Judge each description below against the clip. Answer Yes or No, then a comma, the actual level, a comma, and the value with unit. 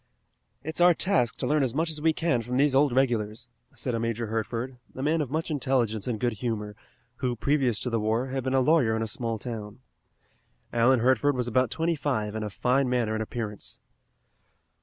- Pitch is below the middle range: Yes, low, 125 Hz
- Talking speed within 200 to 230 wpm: Yes, fast, 205 wpm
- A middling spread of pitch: Yes, average, 3.7 semitones